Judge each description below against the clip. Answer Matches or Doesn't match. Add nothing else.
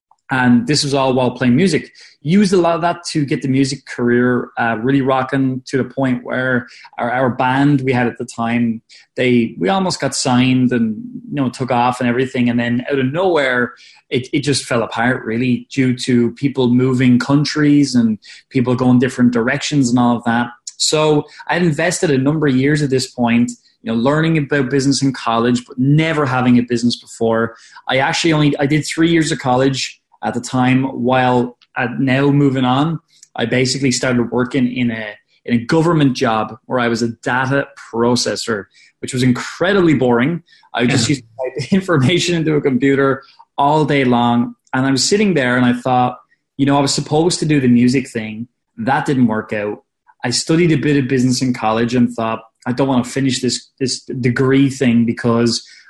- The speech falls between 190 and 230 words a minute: Matches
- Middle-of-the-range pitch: Doesn't match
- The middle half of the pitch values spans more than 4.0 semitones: Doesn't match